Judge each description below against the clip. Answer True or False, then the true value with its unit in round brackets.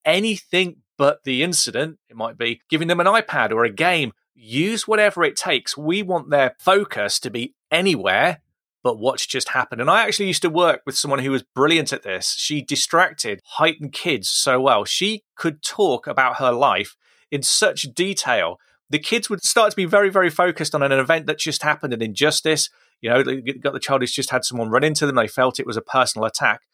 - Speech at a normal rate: False (210 wpm)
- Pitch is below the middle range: False (155 Hz)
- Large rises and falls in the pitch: False (4.8 semitones)